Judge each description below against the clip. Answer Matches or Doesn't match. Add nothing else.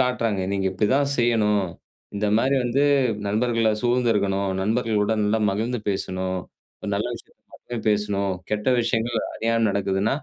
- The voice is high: Doesn't match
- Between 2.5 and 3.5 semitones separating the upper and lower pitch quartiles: Matches